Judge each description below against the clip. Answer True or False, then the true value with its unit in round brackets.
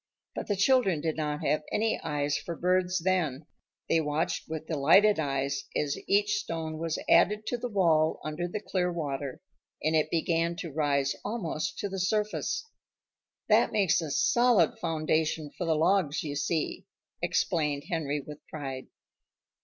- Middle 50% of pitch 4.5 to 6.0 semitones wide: False (4.0 semitones)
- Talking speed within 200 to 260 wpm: False (155 wpm)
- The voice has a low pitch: False (160 Hz)